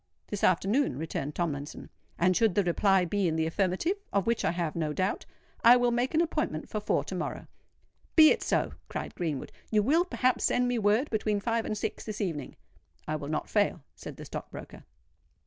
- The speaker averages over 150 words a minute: Yes, average, 195 wpm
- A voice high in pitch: Yes, high, 205 Hz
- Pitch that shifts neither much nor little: No, wide, 5.9 semitones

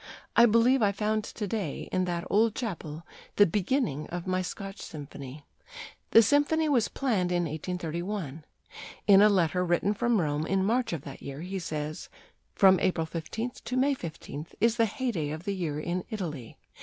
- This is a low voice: No, medium, 185 Hz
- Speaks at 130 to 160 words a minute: No, average, 175 wpm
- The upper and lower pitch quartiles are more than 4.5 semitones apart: Yes, wide, 5.4 semitones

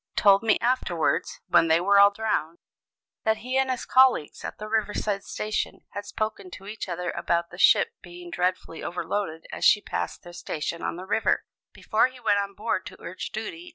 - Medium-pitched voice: No, high, 200 Hz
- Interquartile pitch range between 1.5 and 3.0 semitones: No, average, 3.7 semitones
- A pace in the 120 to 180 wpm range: No, average, 195 wpm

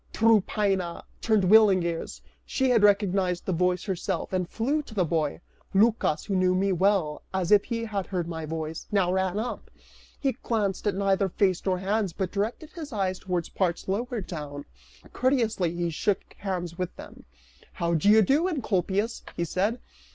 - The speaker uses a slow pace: No, average, 175 wpm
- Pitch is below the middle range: No, high, 195 Hz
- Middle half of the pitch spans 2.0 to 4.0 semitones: Yes, average, 3.4 semitones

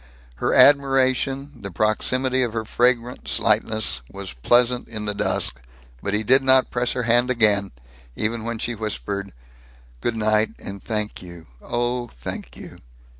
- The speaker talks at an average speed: Yes, average, 150 wpm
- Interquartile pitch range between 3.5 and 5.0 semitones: No, average, 3.1 semitones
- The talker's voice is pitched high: No, low, 115 Hz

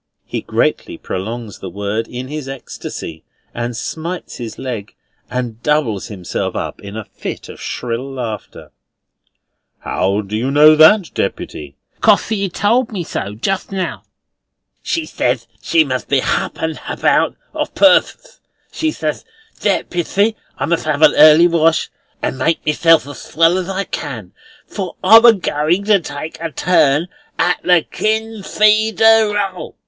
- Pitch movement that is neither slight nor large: No, wide, 7.9 semitones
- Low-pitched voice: No, medium, 155 Hz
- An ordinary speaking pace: Yes, average, 155 wpm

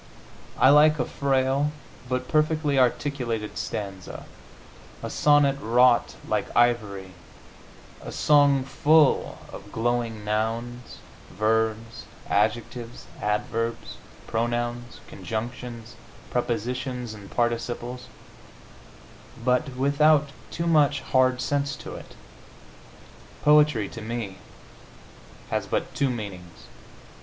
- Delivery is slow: Yes, slow, 95 wpm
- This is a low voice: Yes, low, 120 Hz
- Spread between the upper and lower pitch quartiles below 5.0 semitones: Yes, average, 3.7 semitones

